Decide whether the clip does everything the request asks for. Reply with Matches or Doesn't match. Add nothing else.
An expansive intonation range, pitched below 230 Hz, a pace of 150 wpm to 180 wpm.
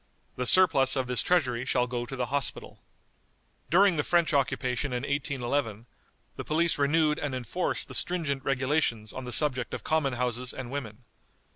Doesn't match